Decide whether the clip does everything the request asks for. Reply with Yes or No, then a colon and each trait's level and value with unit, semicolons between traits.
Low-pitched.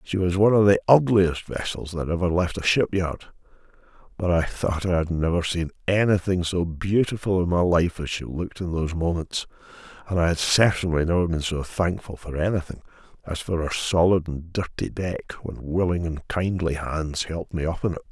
Yes: very low, 85 Hz